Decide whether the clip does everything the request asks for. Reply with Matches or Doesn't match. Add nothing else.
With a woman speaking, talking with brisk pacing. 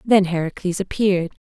Doesn't match